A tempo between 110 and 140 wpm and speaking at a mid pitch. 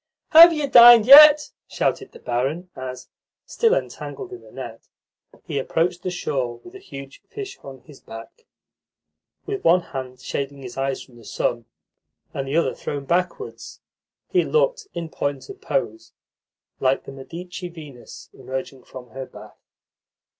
No: average, 155 wpm; medium, 165 Hz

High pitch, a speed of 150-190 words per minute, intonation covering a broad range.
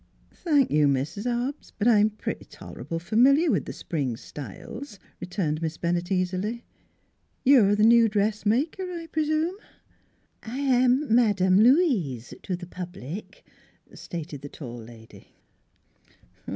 No: high, 210 Hz; average, 140 wpm; wide, 7.2 semitones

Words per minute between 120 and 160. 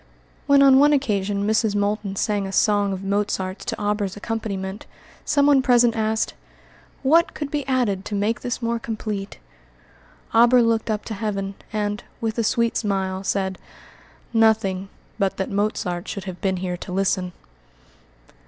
Yes: average, 155 wpm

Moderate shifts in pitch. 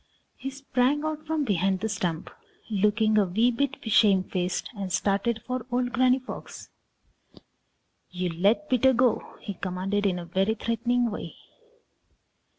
Yes: average, 4.6 semitones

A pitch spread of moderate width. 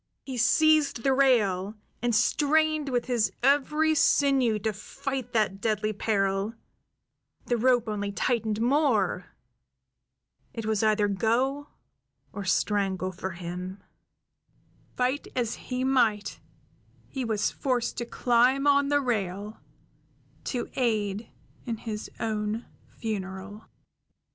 Yes: average, 4.1 semitones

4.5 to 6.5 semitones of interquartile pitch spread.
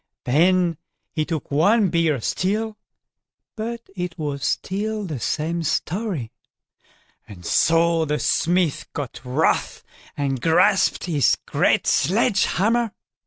Yes: average, 4.9 semitones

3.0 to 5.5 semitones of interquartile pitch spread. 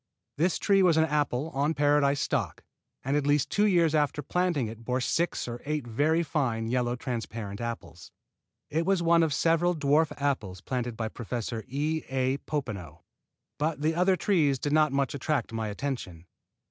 Yes: average, 4.9 semitones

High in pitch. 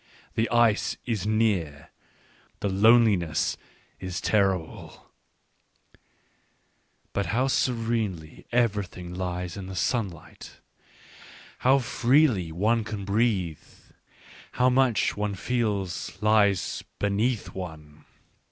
No: low, 105 Hz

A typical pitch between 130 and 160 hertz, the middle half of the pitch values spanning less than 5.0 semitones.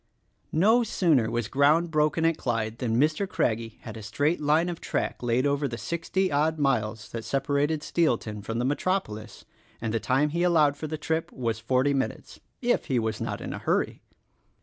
No: medium, 140 Hz; wide, 5.6 semitones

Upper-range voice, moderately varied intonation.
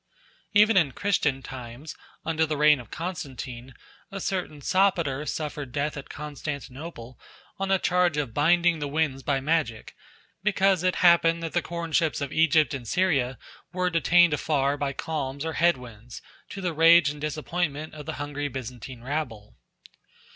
No: medium, 150 Hz; average, 3.9 semitones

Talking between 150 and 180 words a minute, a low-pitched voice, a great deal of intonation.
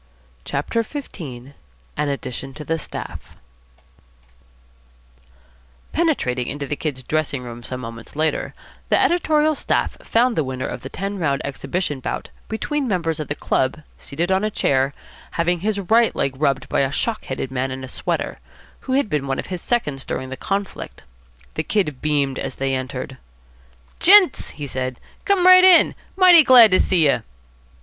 No: average, 165 wpm; medium, 150 Hz; wide, 8.4 semitones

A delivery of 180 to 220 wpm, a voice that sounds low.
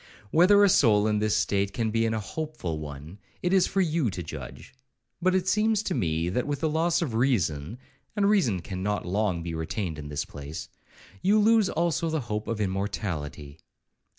Yes: average, 190 wpm; low, 110 Hz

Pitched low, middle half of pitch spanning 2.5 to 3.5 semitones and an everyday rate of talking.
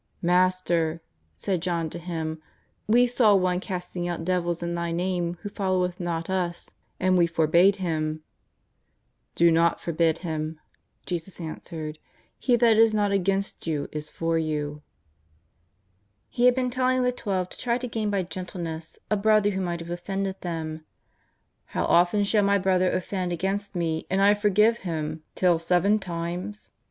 No: medium, 180 Hz; average, 3.1 semitones; average, 165 wpm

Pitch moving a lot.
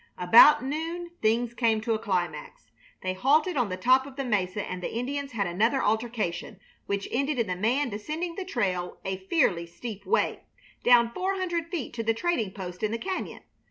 Yes: wide, 6.6 semitones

